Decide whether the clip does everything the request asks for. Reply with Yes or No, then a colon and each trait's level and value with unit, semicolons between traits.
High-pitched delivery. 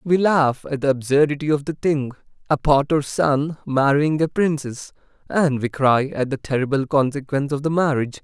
No: medium, 145 Hz